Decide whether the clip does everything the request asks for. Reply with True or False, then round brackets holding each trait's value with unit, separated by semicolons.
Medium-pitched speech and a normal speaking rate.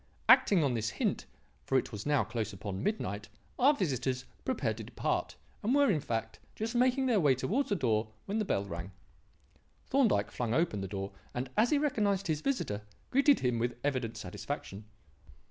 False (130 Hz; 180 wpm)